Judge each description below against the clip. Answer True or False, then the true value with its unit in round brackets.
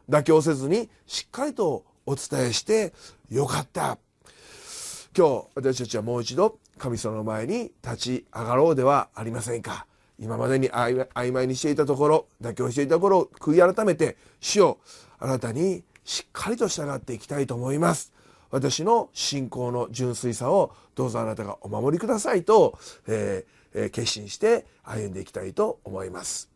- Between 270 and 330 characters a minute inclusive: True (320 characters per minute)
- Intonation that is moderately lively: True (5.0 semitones)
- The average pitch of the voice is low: True (130 Hz)